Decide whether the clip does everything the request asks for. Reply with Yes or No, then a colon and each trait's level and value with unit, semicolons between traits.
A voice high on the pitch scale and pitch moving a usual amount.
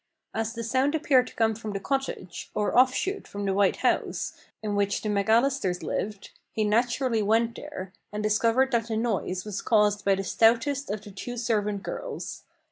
Yes: high, 220 Hz; average, 3.2 semitones